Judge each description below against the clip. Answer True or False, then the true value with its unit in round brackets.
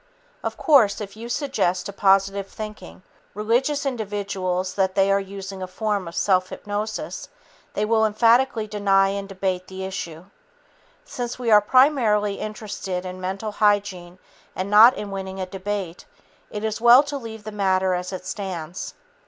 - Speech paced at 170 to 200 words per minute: False (160 wpm)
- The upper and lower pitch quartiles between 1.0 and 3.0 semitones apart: True (2.4 semitones)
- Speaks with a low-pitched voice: False (200 Hz)